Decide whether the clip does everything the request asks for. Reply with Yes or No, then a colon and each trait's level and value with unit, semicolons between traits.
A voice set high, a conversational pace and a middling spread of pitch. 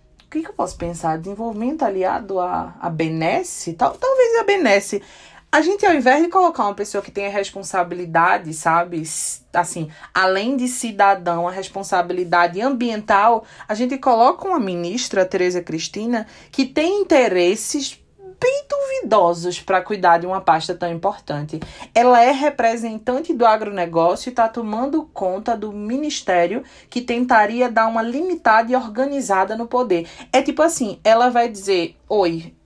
No: high, 215 Hz; average, 145 wpm; wide, 6.3 semitones